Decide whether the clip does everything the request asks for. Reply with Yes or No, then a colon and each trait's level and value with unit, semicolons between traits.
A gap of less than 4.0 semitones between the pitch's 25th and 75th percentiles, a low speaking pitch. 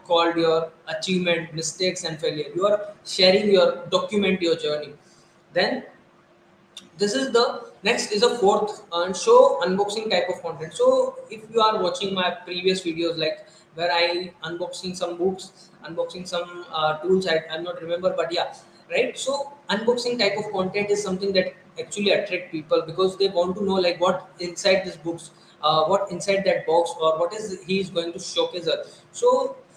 No: average, 3.0 semitones; medium, 185 Hz